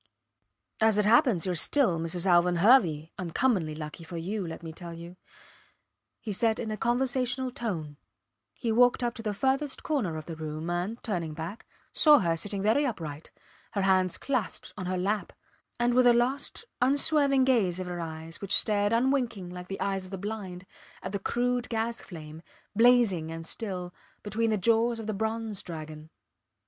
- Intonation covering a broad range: Yes, wide, 5.7 semitones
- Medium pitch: No, high, 200 Hz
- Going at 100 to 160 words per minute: No, average, 180 wpm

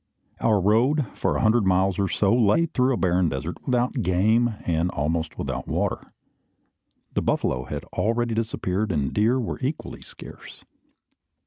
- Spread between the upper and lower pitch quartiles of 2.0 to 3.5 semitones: No, average, 4.9 semitones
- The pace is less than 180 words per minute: Yes, average, 150 wpm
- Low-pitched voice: Yes, low, 105 Hz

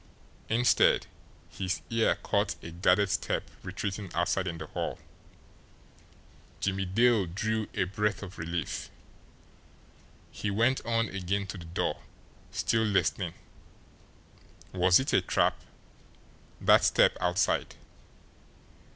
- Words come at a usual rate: No, slow, 110 wpm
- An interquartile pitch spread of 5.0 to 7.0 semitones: No, average, 3.4 semitones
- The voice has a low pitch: Yes, low, 100 Hz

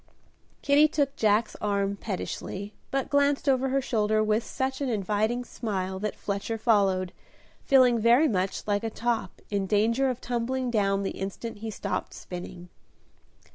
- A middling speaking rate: Yes, average, 150 wpm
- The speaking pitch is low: No, high, 220 Hz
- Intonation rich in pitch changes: No, average, 4.2 semitones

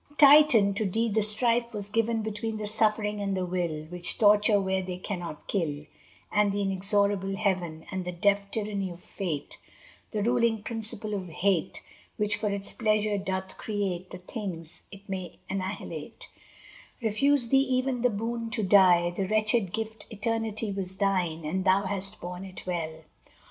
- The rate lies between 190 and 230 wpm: No, average, 165 wpm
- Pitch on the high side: Yes, high, 200 Hz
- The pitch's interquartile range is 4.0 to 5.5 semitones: No, average, 2.9 semitones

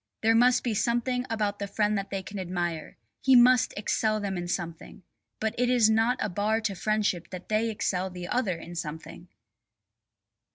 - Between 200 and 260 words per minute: No, average, 180 wpm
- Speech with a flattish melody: No, average, 3.8 semitones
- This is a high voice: Yes, high, 210 Hz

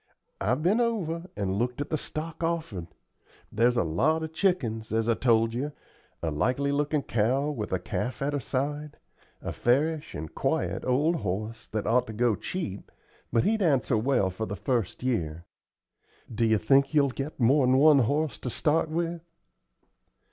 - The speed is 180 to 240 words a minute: No, average, 170 wpm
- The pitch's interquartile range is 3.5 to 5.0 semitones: No, wide, 5.6 semitones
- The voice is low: Yes, low, 130 Hz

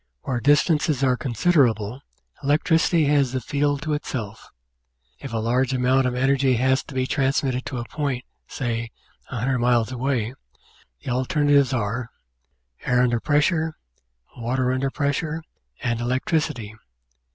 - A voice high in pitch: No, low, 130 Hz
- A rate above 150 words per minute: No, slow, 135 wpm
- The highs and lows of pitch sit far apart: No, average, 2.9 semitones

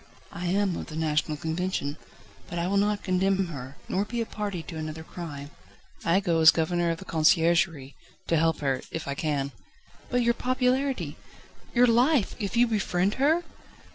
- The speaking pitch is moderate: Yes, medium, 175 Hz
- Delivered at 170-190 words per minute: Yes, average, 175 wpm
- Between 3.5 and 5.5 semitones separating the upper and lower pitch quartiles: Yes, average, 4.6 semitones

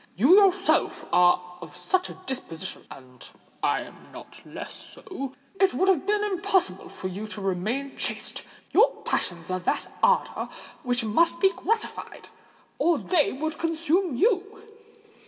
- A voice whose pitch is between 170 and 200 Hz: No, very high, 290 Hz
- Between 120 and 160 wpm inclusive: Yes, average, 140 wpm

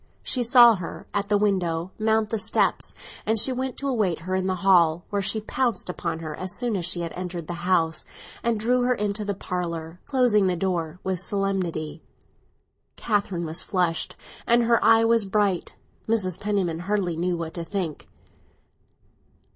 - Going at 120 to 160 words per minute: No, average, 170 wpm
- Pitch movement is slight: No, average, 4.0 semitones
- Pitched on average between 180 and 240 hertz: Yes, high, 190 Hz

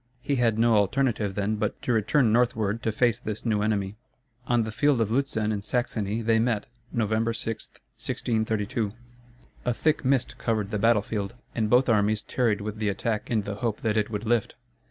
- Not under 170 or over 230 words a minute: Yes, average, 190 wpm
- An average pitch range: No, narrow, 2.0 semitones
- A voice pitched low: Yes, low, 110 Hz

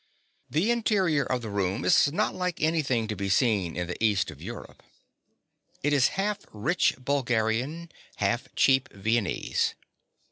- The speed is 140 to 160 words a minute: Yes, average, 145 wpm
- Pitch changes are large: Yes, wide, 6.8 semitones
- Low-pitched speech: Yes, low, 125 Hz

